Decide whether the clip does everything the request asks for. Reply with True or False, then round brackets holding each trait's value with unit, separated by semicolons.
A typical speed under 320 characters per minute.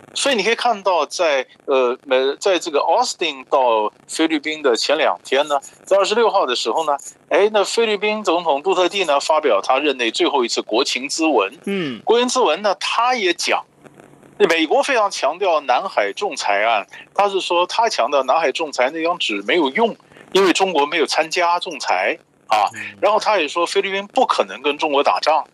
True (285 characters per minute)